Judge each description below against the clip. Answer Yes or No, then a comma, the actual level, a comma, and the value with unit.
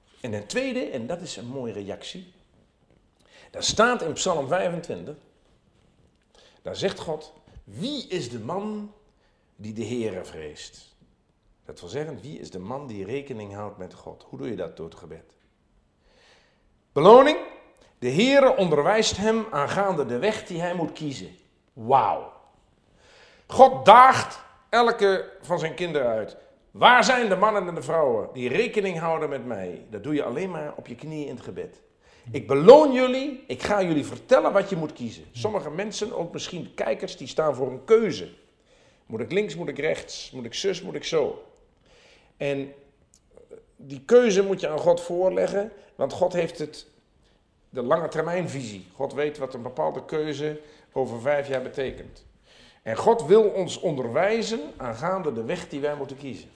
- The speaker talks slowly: No, average, 165 wpm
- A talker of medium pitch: Yes, medium, 175 Hz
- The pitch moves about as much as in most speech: No, wide, 8.5 semitones